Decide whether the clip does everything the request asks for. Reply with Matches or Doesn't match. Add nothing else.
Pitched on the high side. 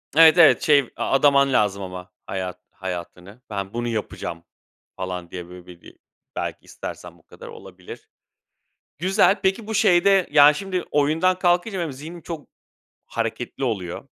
Doesn't match